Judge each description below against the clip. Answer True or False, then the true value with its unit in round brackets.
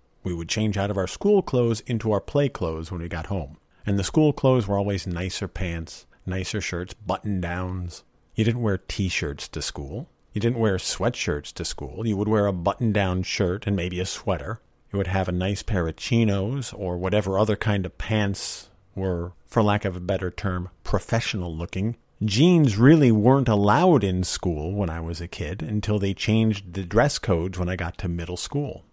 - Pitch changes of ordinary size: True (3.5 semitones)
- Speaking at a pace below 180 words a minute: False (205 wpm)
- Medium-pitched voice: False (100 Hz)